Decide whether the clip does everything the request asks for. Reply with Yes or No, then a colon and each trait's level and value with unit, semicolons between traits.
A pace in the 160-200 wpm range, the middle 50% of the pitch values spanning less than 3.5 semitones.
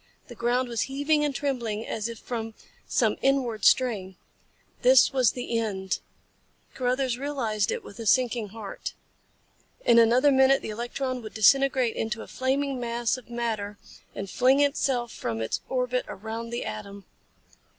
No: average, 150 wpm; average, 3.1 semitones